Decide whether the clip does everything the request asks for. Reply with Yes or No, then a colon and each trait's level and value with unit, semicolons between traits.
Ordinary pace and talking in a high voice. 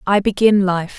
Yes: average, 180 wpm; high, 195 Hz